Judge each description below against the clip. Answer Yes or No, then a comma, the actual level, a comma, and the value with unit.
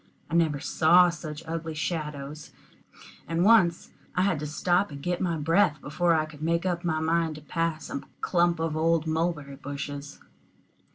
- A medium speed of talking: Yes, average, 165 wpm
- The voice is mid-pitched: Yes, medium, 160 Hz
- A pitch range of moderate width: No, narrow, 2.2 semitones